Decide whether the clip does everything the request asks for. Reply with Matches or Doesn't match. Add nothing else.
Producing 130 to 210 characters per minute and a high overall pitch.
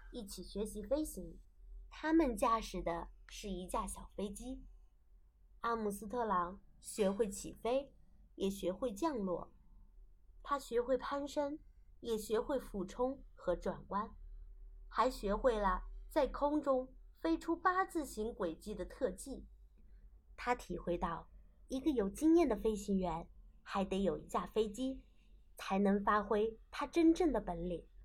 Matches